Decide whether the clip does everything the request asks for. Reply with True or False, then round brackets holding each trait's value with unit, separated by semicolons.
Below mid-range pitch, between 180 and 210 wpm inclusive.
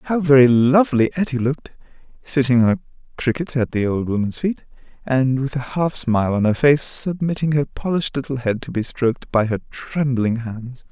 True (130 Hz; 185 wpm)